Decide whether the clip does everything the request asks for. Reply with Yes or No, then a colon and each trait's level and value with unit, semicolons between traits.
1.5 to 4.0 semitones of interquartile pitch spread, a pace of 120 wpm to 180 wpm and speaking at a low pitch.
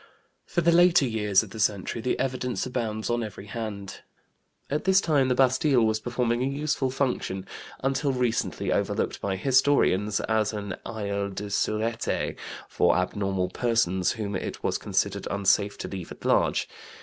No: average, 4.4 semitones; average, 160 wpm; low, 115 Hz